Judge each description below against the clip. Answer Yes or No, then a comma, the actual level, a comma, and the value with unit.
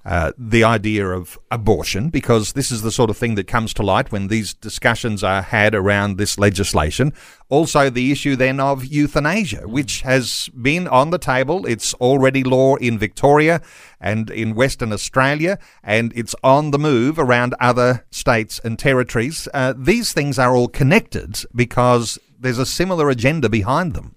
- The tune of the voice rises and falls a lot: No, average, 3.8 semitones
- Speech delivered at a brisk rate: No, average, 170 wpm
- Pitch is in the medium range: No, low, 125 Hz